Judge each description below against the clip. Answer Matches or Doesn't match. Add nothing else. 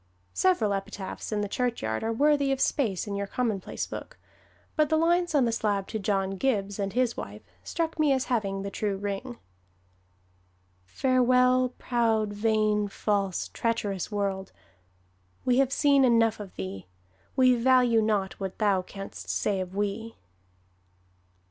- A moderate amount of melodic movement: Matches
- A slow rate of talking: Doesn't match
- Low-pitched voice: Doesn't match